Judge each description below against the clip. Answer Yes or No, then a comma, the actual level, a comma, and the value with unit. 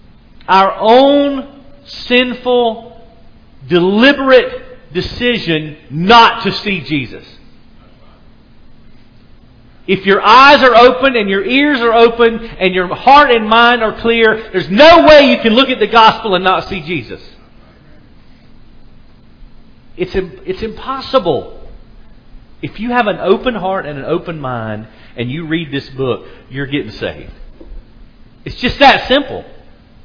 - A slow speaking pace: Yes, slow, 130 wpm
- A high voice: Yes, high, 195 Hz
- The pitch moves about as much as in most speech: No, wide, 8.2 semitones